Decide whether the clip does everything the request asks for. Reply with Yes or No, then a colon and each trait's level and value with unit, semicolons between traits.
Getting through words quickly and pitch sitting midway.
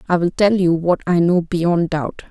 Yes: fast, 235 wpm; medium, 175 Hz